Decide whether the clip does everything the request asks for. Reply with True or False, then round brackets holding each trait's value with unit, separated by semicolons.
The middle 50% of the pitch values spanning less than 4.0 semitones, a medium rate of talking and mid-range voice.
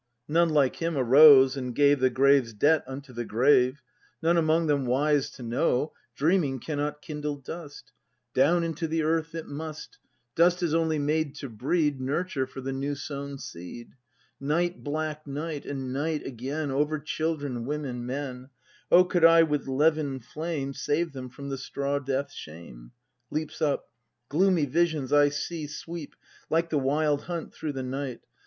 True (2.9 semitones; 160 wpm; 145 Hz)